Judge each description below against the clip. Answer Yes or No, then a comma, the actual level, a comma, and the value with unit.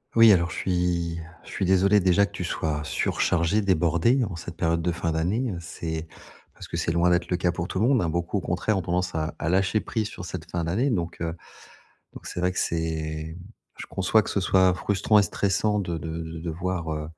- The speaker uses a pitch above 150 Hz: No, very low, 90 Hz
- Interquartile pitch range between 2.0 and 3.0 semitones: Yes, narrow, 2.6 semitones